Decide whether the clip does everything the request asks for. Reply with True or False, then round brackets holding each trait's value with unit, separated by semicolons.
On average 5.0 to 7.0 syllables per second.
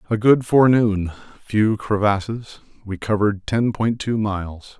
False (4.5 syllables/s)